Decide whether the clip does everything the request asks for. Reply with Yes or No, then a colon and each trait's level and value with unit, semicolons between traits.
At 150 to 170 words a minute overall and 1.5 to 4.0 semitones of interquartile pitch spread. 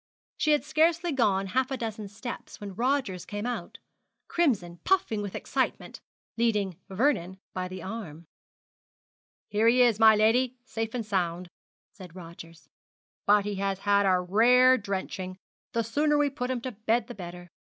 No: average, 160 wpm; average, 4.9 semitones